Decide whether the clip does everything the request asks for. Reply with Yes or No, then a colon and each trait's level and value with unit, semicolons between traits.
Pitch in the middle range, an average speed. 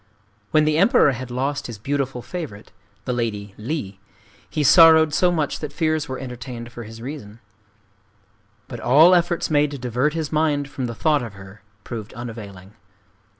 No: low, 130 Hz; average, 165 wpm